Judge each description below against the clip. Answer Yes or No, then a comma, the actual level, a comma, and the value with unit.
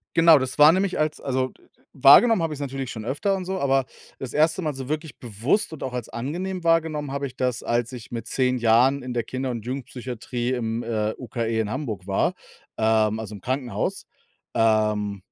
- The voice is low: Yes, low, 130 Hz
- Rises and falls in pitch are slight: No, average, 4.4 semitones